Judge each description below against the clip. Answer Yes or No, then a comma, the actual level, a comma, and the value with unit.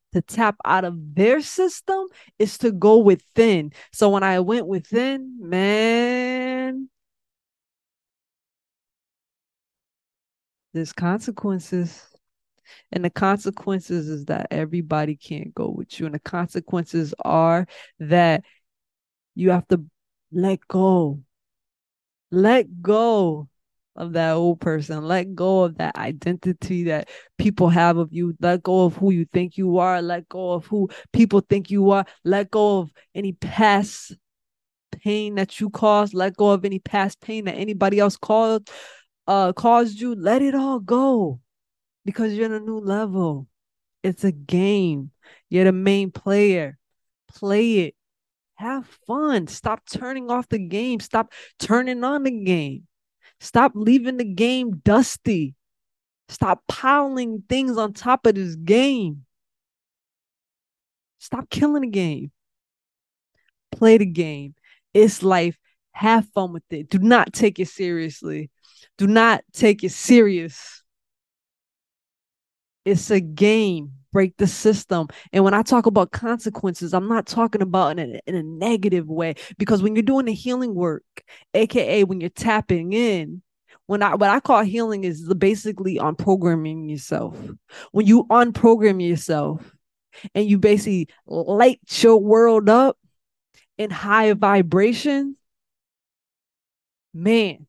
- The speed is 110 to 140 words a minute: Yes, slow, 135 wpm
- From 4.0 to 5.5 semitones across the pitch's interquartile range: Yes, average, 4.3 semitones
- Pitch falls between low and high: No, high, 195 Hz